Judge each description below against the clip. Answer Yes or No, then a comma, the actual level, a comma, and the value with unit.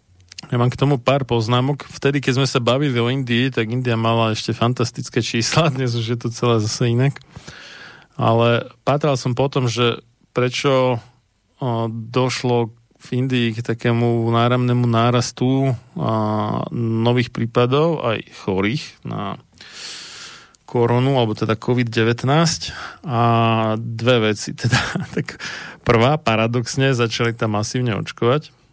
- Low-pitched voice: Yes, low, 120 Hz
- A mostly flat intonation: Yes, narrow, 2.1 semitones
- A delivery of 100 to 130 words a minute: Yes, average, 120 wpm